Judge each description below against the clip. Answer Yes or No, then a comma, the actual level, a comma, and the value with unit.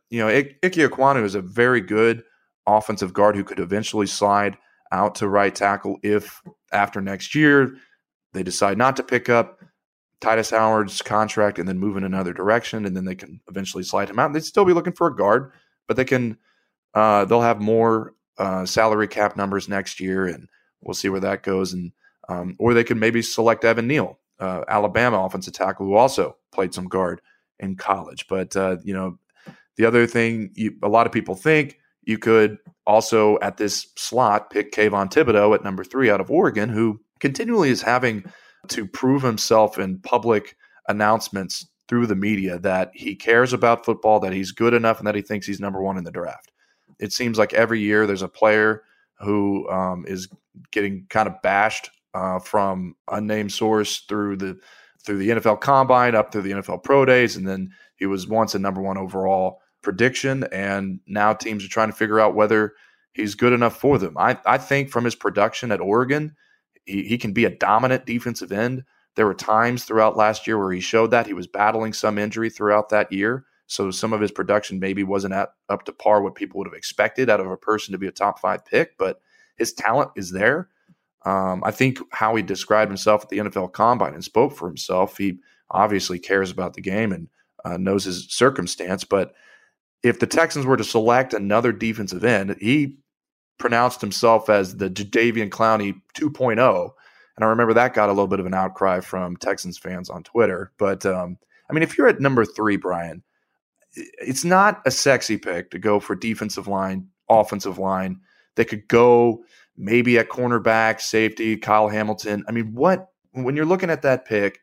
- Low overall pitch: Yes, low, 105 Hz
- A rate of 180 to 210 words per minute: Yes, average, 195 wpm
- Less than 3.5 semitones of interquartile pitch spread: Yes, average, 3.1 semitones